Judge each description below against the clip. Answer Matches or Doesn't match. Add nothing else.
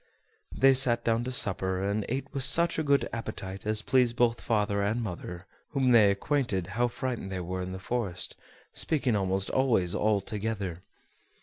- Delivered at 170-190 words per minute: Matches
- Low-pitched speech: Matches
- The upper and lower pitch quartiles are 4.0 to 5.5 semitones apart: Matches